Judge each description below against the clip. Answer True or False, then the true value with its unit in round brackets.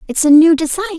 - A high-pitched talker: True (325 Hz)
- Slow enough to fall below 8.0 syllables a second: False (8.7 syllables/s)